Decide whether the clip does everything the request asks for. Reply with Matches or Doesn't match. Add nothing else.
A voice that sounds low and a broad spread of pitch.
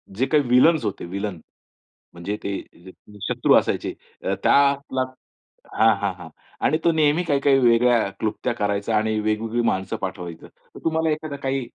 Matches